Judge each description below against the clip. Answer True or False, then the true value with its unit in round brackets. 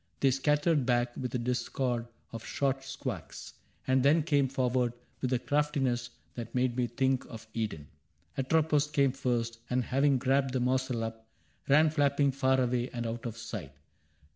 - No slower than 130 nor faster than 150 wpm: False (165 wpm)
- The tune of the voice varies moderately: False (2.3 semitones)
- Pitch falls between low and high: False (130 Hz)